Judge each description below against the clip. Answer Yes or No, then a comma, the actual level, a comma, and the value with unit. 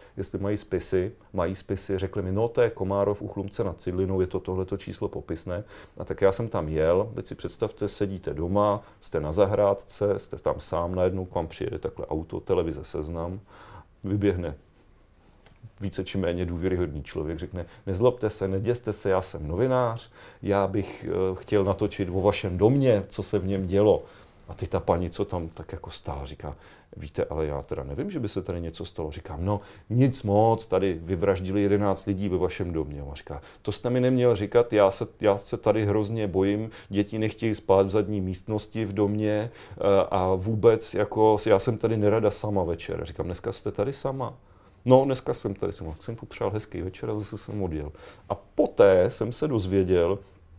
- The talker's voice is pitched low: Yes, low, 100 Hz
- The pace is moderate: No, fast, 185 wpm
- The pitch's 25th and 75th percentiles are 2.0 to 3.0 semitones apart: Yes, narrow, 2.5 semitones